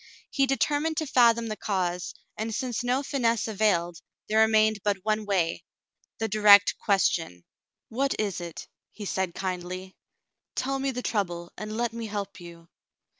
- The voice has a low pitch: No, high, 215 Hz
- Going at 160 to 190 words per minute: Yes, average, 170 wpm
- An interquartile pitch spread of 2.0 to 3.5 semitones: No, average, 4.0 semitones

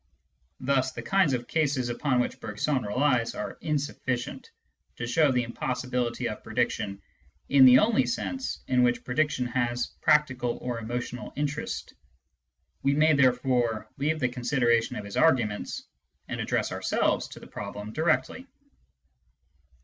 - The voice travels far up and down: No, average, 3.3 semitones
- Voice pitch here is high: No, low, 125 Hz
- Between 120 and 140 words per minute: Yes, slow, 135 wpm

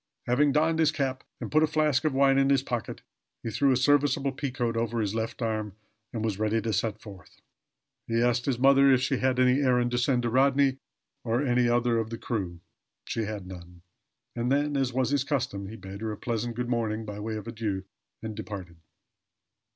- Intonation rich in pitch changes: No, average, 3.7 semitones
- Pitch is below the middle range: Yes, low, 120 Hz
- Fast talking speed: Yes, fast, 210 wpm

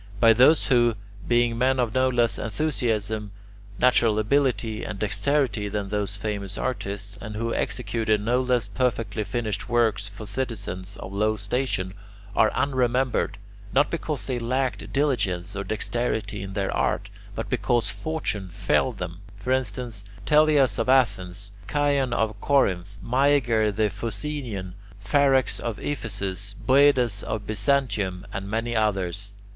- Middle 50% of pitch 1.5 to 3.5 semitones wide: No, average, 4.1 semitones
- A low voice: Yes, low, 110 Hz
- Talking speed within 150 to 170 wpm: No, slow, 135 wpm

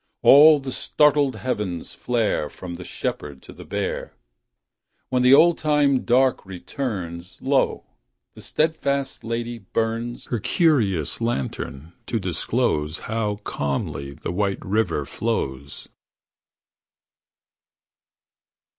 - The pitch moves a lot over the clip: Yes, wide, 7.1 semitones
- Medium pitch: No, low, 115 Hz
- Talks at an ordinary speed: No, slow, 105 wpm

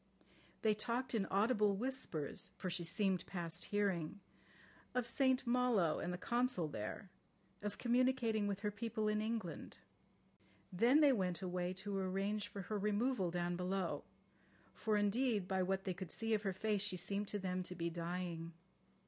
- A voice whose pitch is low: No, high, 200 Hz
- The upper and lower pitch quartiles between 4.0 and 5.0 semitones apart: No, average, 3.6 semitones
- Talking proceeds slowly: No, average, 165 wpm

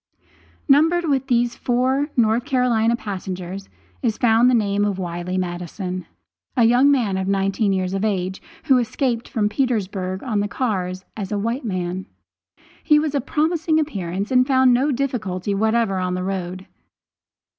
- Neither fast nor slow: Yes, average, 155 wpm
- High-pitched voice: Yes, high, 220 Hz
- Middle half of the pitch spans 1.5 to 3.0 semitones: No, average, 5.1 semitones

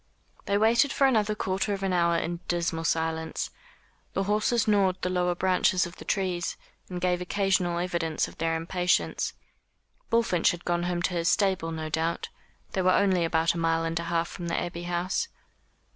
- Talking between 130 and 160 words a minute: No, average, 185 wpm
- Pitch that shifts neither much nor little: No, narrow, 2.3 semitones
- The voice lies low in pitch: No, medium, 175 Hz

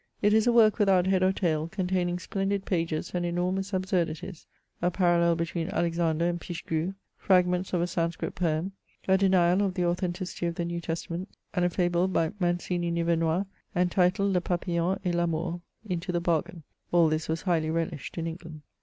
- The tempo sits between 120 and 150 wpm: No, average, 180 wpm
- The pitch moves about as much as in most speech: No, narrow, 1.8 semitones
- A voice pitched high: No, medium, 175 Hz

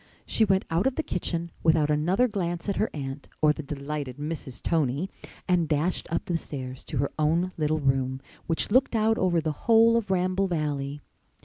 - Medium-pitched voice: Yes, medium, 165 Hz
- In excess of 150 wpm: Yes, average, 190 wpm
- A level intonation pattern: No, average, 4.1 semitones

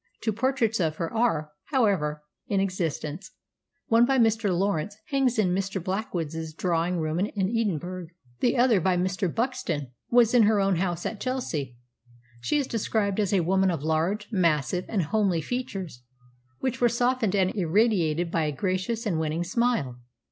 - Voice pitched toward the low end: No, high, 190 Hz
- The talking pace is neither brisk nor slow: Yes, average, 160 wpm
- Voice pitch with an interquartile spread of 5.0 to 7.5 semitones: Yes, wide, 5.4 semitones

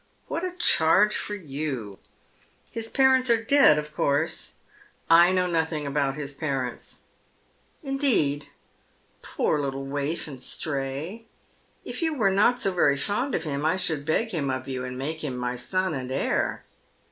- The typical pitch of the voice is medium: Yes, medium, 155 Hz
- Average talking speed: Yes, average, 170 wpm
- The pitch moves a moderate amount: No, wide, 6.9 semitones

